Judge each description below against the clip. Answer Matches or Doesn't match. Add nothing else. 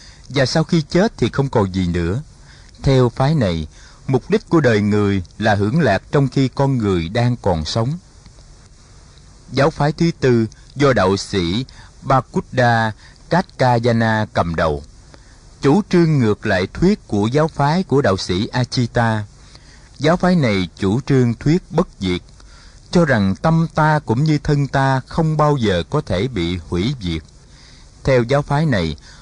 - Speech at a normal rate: Doesn't match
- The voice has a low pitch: Matches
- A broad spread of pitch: Matches